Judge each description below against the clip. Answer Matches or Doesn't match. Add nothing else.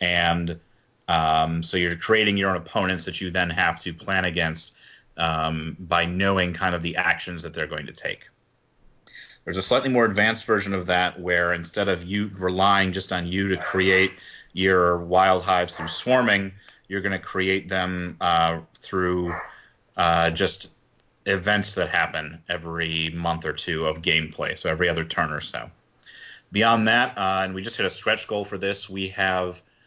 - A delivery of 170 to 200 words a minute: Matches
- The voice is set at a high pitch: Doesn't match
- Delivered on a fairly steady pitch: Matches